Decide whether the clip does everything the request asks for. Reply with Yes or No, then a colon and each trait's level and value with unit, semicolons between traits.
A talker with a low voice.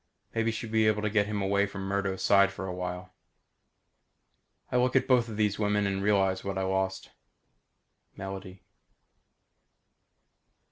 Yes: low, 100 Hz